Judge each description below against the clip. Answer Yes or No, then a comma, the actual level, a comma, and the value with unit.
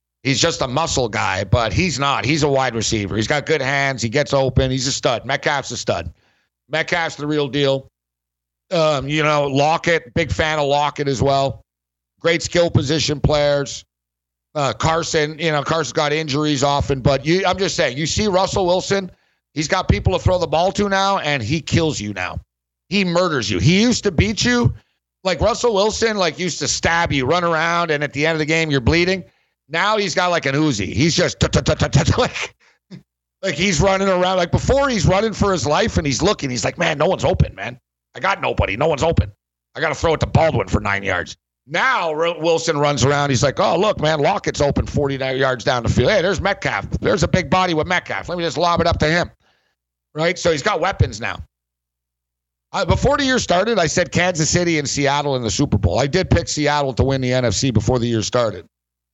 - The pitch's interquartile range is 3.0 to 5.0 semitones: No, wide, 5.5 semitones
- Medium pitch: Yes, medium, 145 Hz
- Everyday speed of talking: No, fast, 215 wpm